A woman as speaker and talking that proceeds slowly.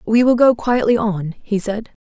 No: female; fast, 205 wpm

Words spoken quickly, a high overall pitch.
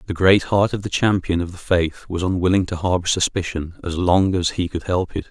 No: fast, 240 wpm; very low, 90 Hz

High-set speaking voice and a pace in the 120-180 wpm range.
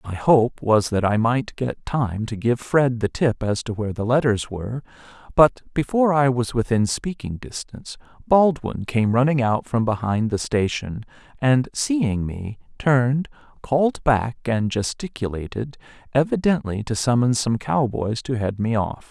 No: low, 120 Hz; average, 160 wpm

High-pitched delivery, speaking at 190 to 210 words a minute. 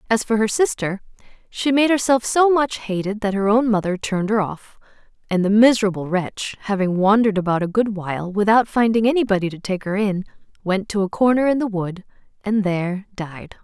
Yes: high, 210 Hz; average, 195 wpm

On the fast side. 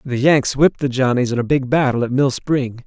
Yes: fast, 250 wpm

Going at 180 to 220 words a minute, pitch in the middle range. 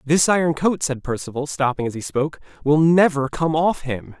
Yes: average, 200 wpm; medium, 150 Hz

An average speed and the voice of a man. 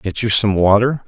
No: fast, 225 wpm; male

